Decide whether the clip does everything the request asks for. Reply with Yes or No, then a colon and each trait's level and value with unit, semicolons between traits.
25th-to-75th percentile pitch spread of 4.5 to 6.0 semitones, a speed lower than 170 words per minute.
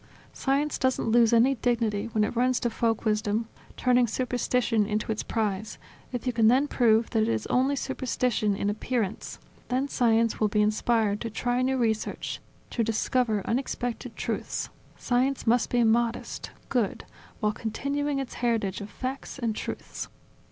No: narrow, 2.6 semitones; average, 160 wpm